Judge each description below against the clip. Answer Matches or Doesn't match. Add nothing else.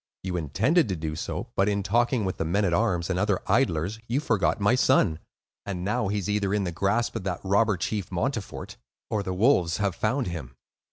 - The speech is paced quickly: Matches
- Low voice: Matches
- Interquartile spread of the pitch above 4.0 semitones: Doesn't match